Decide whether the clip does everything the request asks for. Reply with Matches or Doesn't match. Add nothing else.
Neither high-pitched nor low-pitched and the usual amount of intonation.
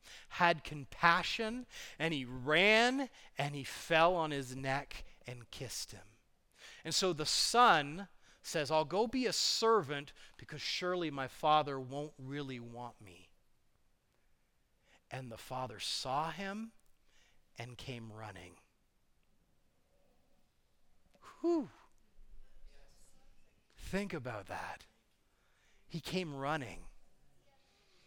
Doesn't match